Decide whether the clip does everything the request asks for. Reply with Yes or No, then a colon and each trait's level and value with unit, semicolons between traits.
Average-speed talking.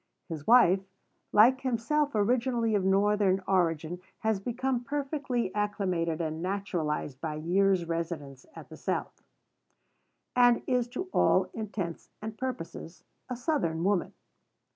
No: slow, 120 wpm